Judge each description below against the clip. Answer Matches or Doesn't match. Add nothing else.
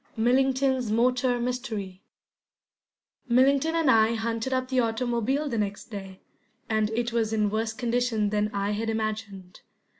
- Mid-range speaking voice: Doesn't match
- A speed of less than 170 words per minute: Matches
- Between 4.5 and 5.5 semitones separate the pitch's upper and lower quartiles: Doesn't match